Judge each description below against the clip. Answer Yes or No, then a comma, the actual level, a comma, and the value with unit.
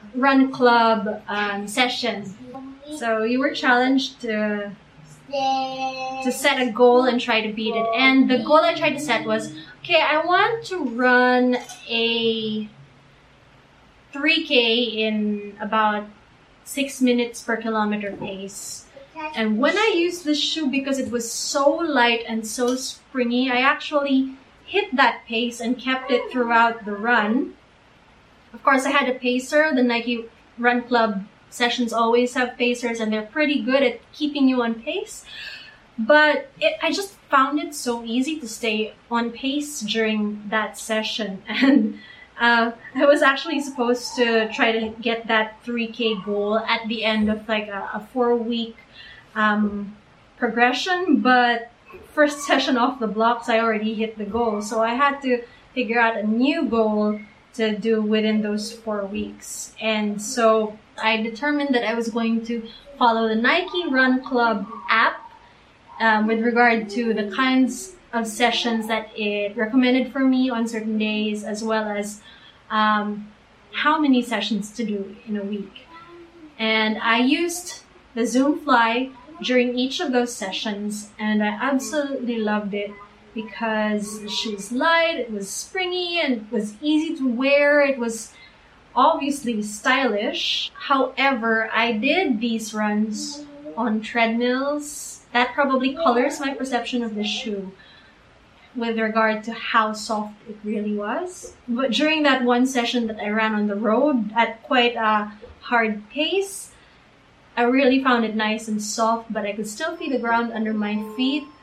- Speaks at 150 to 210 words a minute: Yes, average, 155 wpm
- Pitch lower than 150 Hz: No, high, 235 Hz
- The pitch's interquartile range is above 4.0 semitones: No, average, 3.5 semitones